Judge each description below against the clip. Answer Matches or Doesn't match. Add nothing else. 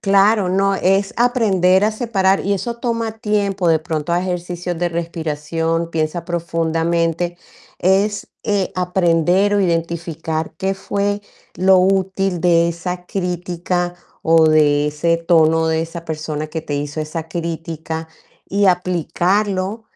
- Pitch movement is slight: Doesn't match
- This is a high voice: Doesn't match